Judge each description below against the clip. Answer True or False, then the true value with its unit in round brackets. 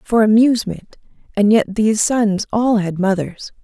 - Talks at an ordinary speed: True (150 wpm)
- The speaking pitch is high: True (210 Hz)